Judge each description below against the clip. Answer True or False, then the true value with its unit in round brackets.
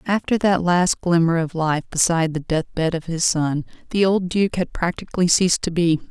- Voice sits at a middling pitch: True (170 Hz)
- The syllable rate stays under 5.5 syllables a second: True (5.1 syllables/s)